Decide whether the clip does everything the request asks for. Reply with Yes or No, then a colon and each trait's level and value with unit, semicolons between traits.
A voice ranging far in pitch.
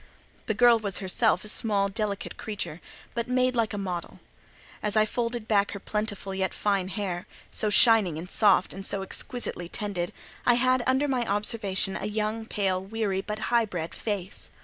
No: average, 2.8 semitones